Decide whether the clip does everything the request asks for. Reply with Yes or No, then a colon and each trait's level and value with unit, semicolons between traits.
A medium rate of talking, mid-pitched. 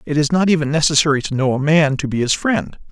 No: fast, 270 wpm; medium, 145 Hz